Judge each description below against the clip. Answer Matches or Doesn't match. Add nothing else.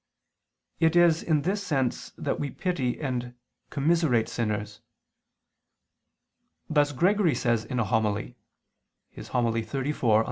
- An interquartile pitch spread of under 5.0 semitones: Doesn't match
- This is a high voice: Doesn't match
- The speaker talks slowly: Matches